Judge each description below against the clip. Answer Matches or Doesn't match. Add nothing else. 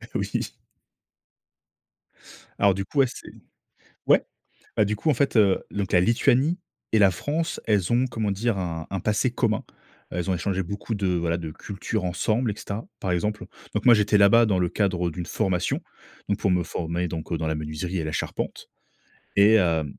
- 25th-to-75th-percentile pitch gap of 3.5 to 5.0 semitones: Matches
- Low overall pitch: Matches